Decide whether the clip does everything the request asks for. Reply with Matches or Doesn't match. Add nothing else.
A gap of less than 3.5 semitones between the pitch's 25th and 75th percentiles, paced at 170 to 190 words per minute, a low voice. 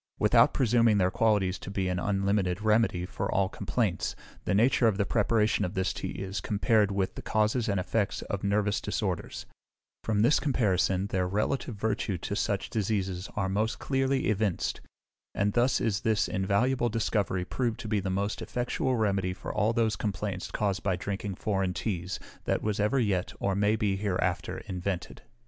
Matches